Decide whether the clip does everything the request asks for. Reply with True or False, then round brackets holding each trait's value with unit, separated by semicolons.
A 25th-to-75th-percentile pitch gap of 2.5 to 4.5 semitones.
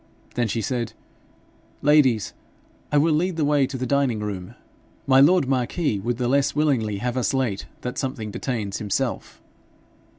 True (4.1 semitones)